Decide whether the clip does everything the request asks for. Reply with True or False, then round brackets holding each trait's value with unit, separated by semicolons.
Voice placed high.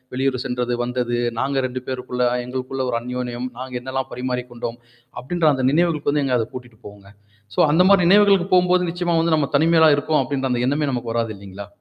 False (130 Hz)